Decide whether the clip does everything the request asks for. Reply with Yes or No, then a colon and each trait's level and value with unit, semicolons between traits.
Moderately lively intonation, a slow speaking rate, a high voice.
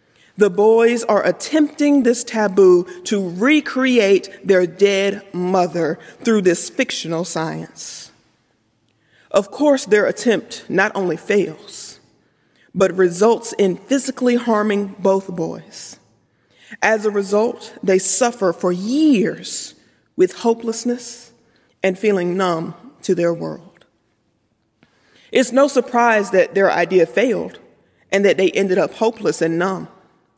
Yes: average, 4.6 semitones; slow, 115 wpm; high, 200 Hz